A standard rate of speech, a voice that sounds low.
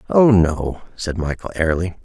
Yes: average, 145 wpm; very low, 90 Hz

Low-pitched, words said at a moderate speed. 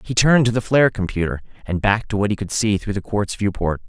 No: low, 105 Hz; fast, 265 wpm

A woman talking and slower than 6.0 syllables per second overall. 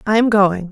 Yes: female; 5.1 syllables/s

